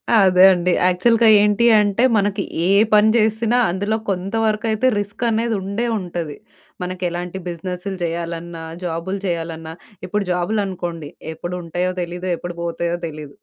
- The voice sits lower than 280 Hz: Yes, medium, 185 Hz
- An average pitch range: Yes, average, 3.3 semitones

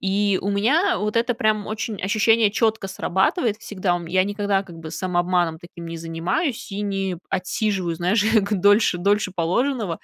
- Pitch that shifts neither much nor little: Yes, average, 3.4 semitones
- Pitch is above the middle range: Yes, high, 200 Hz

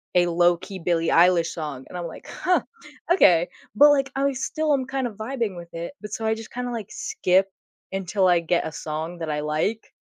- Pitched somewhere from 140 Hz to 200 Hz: Yes, medium, 185 Hz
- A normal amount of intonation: No, wide, 6.6 semitones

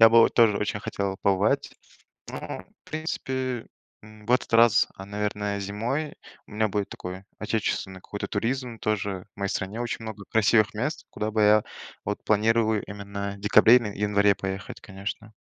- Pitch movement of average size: No, narrow, 2.1 semitones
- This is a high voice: No, low, 105 Hz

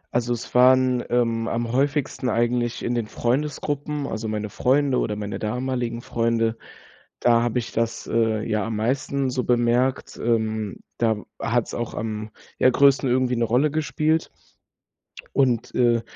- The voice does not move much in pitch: Yes, narrow, 2.2 semitones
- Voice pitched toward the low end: Yes, low, 120 Hz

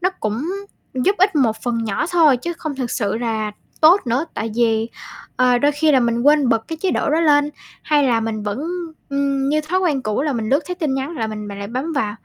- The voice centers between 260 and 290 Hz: Yes, very high, 265 Hz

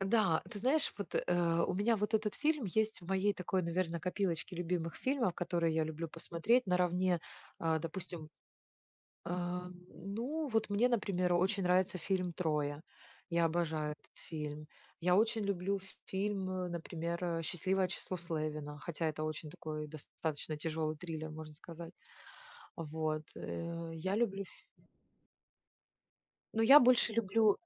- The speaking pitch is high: No, medium, 175 Hz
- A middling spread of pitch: Yes, average, 3.5 semitones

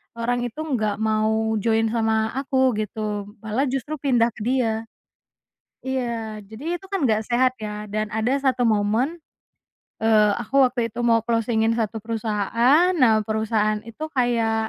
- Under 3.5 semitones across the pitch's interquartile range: Yes, narrow, 2.6 semitones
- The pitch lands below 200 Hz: No, high, 225 Hz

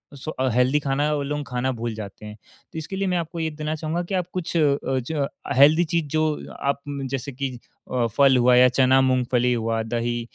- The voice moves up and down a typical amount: Yes, average, 4.0 semitones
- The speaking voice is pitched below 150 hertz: Yes, low, 135 Hz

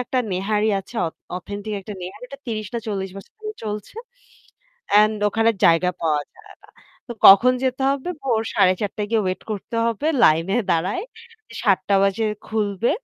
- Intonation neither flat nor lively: Yes, average, 3.3 semitones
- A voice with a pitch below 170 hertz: No, high, 210 Hz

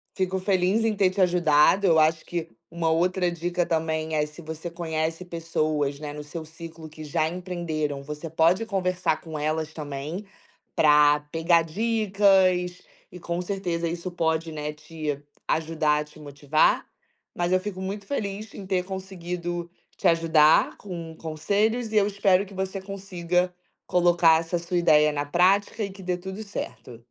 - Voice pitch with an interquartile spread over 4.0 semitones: No, average, 3.0 semitones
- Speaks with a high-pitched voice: No, medium, 170 Hz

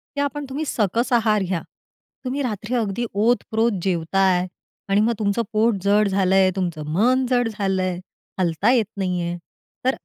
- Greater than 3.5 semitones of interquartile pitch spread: Yes, average, 4.0 semitones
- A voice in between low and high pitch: No, high, 205 Hz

